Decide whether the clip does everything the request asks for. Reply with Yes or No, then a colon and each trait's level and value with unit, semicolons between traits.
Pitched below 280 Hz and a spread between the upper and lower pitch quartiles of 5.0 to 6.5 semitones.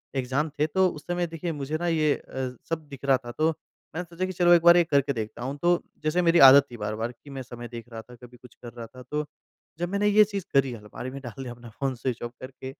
Yes: medium, 140 Hz; average, 5.3 semitones